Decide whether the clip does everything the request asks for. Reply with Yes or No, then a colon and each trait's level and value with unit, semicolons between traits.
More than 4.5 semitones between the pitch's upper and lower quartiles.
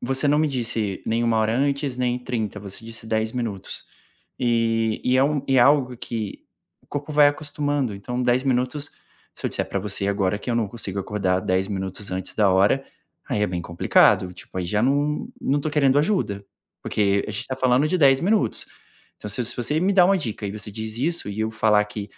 Yes: average, 5.1 semitones